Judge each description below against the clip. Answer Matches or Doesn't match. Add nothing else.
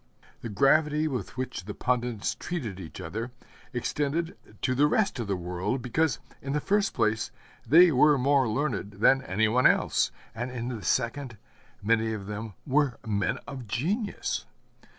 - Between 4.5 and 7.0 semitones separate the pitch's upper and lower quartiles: Matches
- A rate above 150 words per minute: Matches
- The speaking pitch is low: Matches